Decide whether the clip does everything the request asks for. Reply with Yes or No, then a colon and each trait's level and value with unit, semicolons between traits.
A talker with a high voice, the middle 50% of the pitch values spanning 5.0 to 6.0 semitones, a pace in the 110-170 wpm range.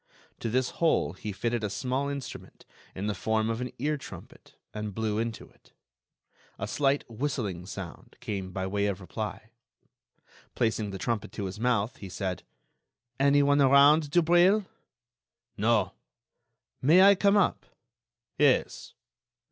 No: low, 115 Hz; wide, 5.5 semitones; average, 140 wpm